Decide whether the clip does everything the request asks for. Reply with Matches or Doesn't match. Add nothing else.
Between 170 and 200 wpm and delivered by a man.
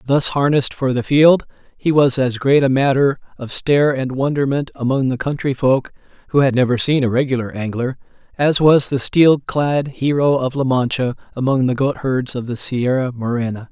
Matches